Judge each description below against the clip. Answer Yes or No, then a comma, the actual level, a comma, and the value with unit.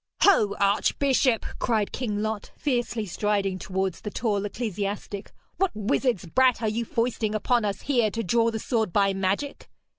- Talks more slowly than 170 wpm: Yes, average, 155 wpm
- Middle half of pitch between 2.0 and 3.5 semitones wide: Yes, average, 3.1 semitones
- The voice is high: Yes, high, 215 Hz